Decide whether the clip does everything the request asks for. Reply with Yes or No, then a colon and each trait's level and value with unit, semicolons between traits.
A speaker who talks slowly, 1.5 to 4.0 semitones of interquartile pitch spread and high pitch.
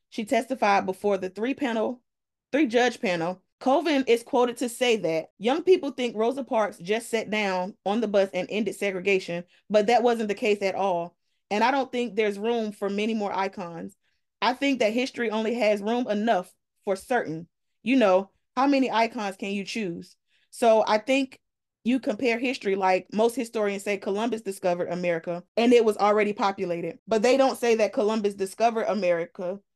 No: average, 180 wpm; average, 3.7 semitones; high, 215 Hz